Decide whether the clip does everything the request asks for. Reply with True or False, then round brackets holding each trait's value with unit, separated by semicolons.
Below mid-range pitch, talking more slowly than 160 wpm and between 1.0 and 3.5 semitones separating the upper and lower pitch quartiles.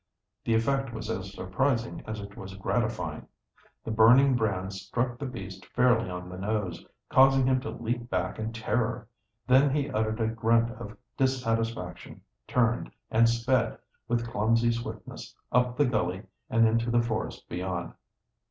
True (115 Hz; 150 wpm; 2.9 semitones)